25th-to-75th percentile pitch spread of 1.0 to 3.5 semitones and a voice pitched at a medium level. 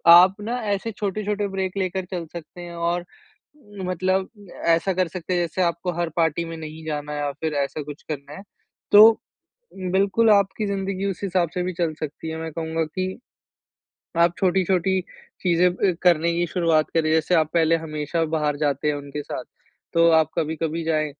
Yes: average, 2.9 semitones; medium, 170 Hz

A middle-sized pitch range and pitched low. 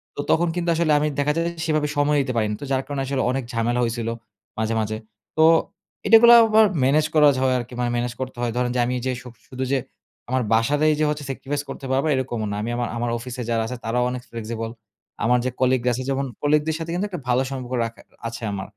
Yes: average, 3.6 semitones; low, 130 Hz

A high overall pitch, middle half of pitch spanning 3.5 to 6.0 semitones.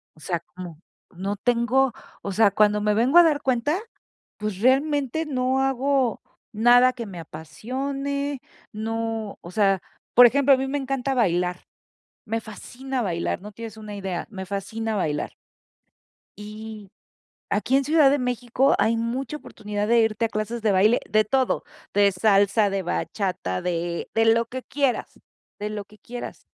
Yes: high, 225 Hz; average, 4.3 semitones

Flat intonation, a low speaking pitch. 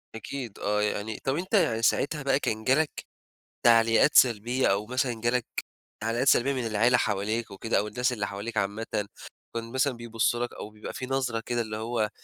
No: average, 3.0 semitones; low, 115 Hz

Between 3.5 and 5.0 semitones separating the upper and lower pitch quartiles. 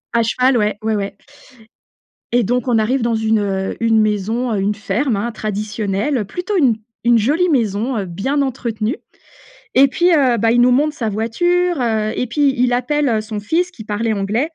Yes: average, 3.8 semitones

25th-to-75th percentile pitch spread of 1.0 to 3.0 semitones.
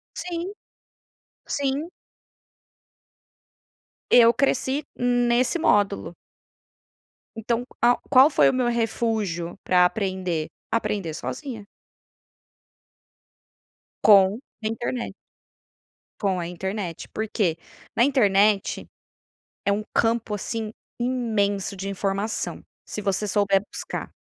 No: average, 3.7 semitones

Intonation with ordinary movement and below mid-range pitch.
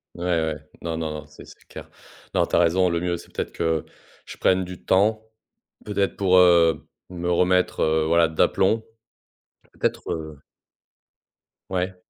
No: narrow, 2.2 semitones; very low, 85 Hz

